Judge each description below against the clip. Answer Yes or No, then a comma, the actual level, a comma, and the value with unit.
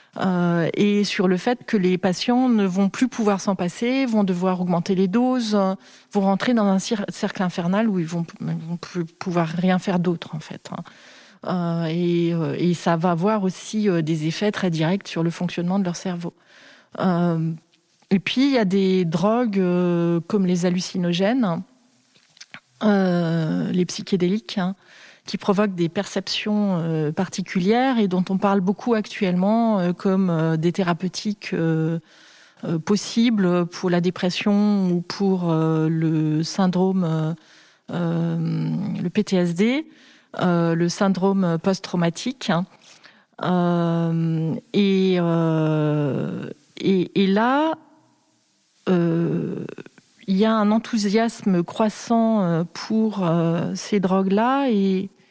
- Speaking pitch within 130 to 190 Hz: Yes, medium, 185 Hz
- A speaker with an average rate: No, slow, 120 wpm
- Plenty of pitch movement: No, average, 3.2 semitones